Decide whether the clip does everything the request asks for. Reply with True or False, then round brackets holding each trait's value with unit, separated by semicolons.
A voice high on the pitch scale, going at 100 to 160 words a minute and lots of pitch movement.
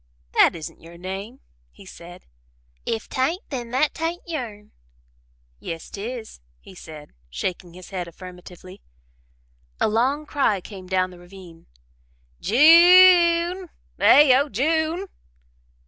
True (220 Hz; 140 wpm; 8.9 semitones)